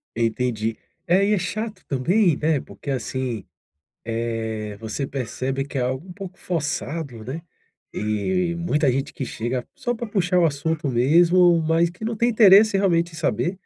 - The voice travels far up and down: Yes, wide, 6.3 semitones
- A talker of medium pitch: Yes, medium, 155 Hz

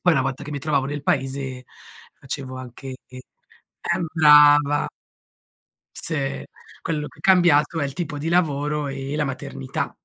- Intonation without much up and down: Yes, narrow, 2.0 semitones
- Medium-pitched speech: Yes, medium, 145 Hz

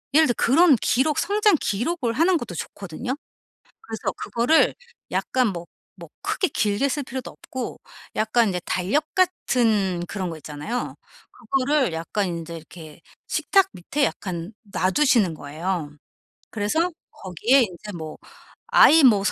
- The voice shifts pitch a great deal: Yes, wide, 7.5 semitones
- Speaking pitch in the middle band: No, high, 225 Hz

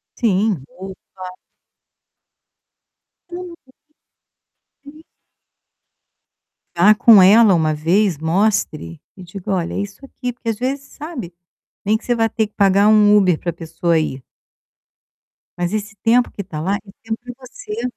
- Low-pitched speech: No, high, 205 Hz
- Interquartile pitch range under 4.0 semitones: No, average, 4.3 semitones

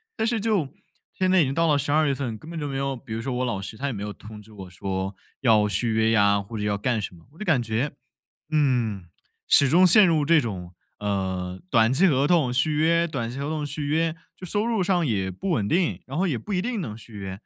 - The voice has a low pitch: Yes, low, 130 Hz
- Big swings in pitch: Yes, wide, 7.4 semitones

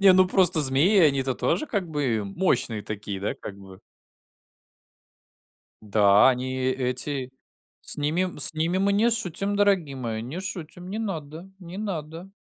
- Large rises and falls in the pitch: Yes, wide, 6.8 semitones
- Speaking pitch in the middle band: Yes, medium, 155 Hz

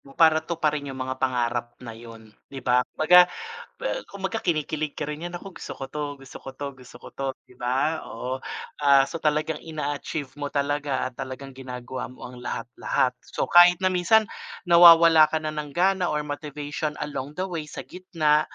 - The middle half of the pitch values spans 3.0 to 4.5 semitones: Yes, average, 3.7 semitones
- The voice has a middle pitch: Yes, medium, 150 Hz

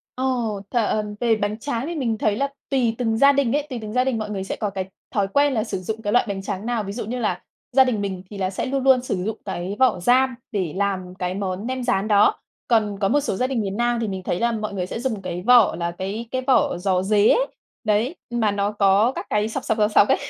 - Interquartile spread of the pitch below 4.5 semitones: Yes, average, 3.9 semitones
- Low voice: No, high, 215 Hz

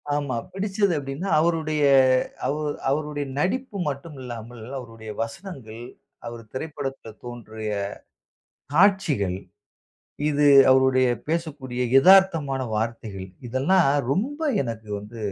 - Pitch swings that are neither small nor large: No, wide, 6.3 semitones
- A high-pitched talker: No, low, 135 Hz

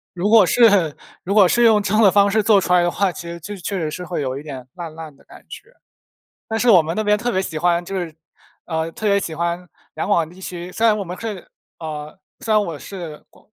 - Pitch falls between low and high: Yes, medium, 180 Hz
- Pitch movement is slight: No, average, 4.0 semitones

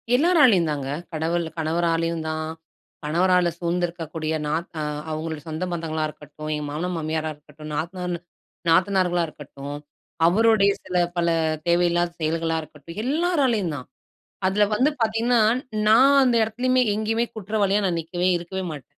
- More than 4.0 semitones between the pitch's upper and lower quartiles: Yes, average, 4.6 semitones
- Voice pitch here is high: No, medium, 175 Hz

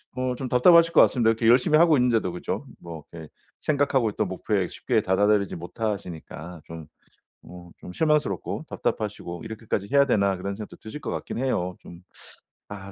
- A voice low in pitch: Yes, low, 105 Hz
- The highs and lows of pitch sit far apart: Yes, wide, 5.9 semitones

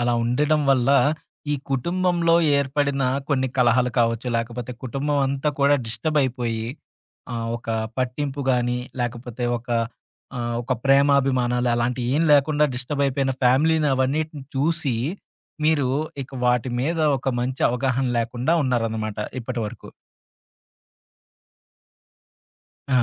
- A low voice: Yes, low, 130 Hz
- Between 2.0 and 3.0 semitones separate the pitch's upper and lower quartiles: Yes, average, 2.7 semitones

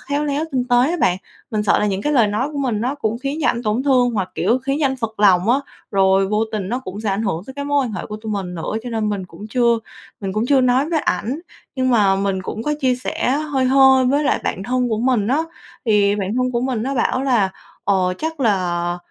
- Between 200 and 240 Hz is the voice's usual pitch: Yes, high, 235 Hz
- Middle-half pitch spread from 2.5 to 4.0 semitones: No, average, 4.7 semitones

